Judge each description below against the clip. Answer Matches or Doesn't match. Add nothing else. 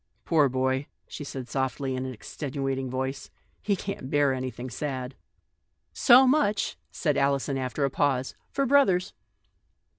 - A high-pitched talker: Doesn't match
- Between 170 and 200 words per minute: Matches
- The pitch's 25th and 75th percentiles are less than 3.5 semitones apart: Matches